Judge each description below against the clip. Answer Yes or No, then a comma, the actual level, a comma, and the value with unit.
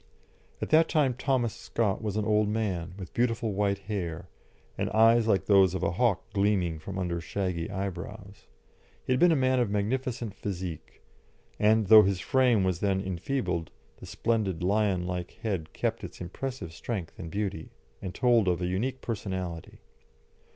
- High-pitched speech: No, low, 100 Hz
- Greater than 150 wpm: Yes, average, 165 wpm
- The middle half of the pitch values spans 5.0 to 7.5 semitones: No, average, 3.9 semitones